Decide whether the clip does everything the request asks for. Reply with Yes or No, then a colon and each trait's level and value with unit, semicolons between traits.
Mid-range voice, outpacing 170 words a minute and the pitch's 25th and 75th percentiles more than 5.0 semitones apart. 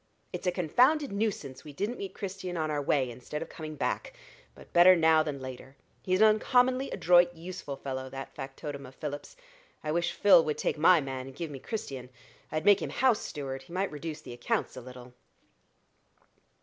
Yes: medium, 155 Hz; average, 190 wpm; wide, 5.4 semitones